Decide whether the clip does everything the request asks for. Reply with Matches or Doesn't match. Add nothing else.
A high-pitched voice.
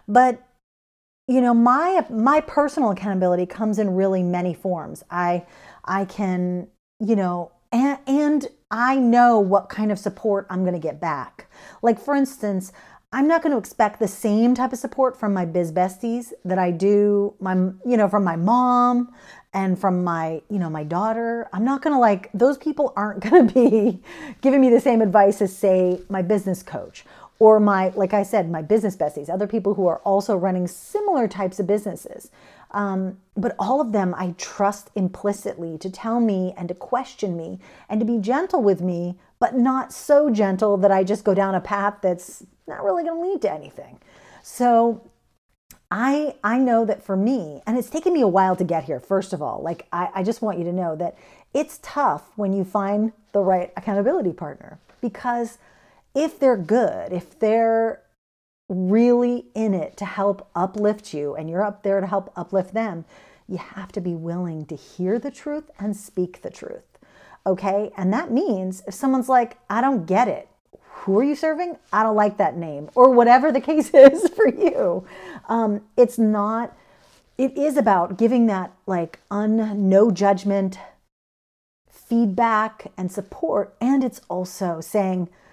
Matches